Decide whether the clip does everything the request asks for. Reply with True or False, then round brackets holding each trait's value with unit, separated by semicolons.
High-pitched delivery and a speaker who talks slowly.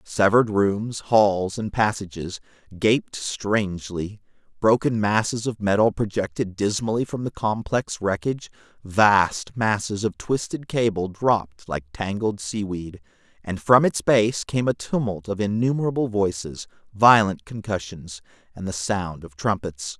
False (105 Hz; 130 wpm)